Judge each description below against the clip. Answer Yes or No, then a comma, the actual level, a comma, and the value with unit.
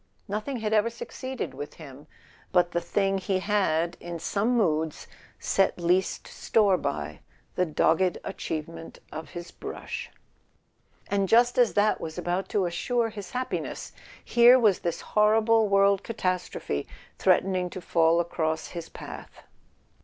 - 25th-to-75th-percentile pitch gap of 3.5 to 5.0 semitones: Yes, average, 4.2 semitones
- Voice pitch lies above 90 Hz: Yes, medium, 185 Hz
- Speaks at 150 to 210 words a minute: No, average, 140 wpm